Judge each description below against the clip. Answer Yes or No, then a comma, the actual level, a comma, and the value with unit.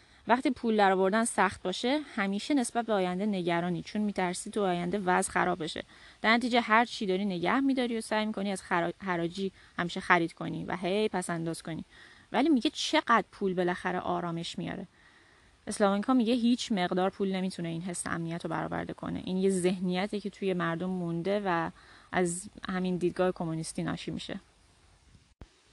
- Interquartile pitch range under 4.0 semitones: Yes, average, 3.5 semitones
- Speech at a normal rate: No, fast, 170 wpm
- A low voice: No, medium, 185 Hz